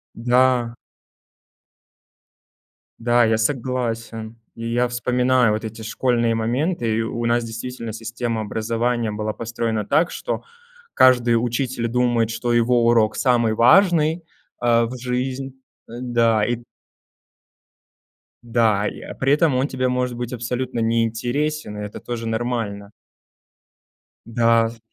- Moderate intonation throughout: No, narrow, 1.8 semitones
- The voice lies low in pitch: Yes, low, 120 Hz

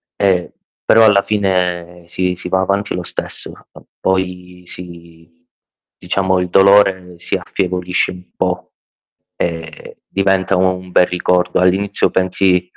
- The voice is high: No, very low, 90 Hz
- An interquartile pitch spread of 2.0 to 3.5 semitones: No, narrow, 1.2 semitones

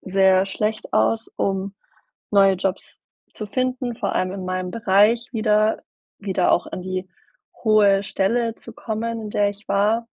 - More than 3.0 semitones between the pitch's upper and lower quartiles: No, average, 2.7 semitones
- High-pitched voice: Yes, high, 205 Hz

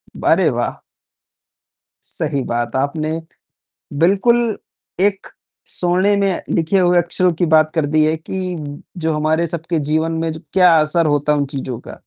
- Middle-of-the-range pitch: Yes, medium, 160 Hz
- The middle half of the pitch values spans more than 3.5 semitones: No, average, 2.9 semitones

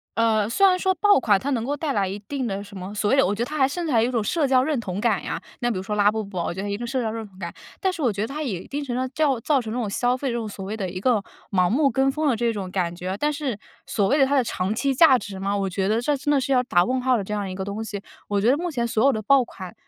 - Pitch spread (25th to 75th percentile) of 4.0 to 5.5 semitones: Yes, average, 5.2 semitones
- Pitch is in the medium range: No, high, 230 Hz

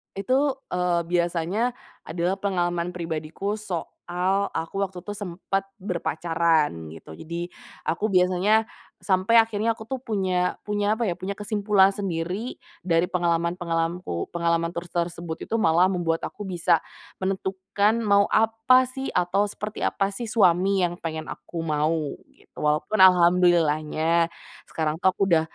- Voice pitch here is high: No, medium, 180 Hz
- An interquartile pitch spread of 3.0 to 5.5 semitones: Yes, average, 3.3 semitones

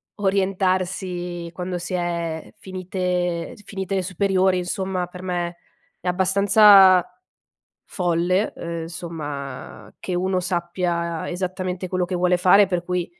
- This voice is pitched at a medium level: Yes, medium, 180 Hz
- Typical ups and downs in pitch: No, narrow, 1.4 semitones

